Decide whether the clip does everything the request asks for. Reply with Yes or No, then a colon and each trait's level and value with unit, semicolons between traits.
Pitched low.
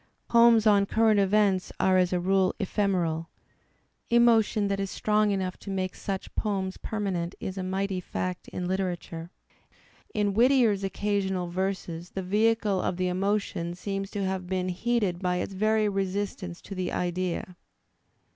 No: high, 195 Hz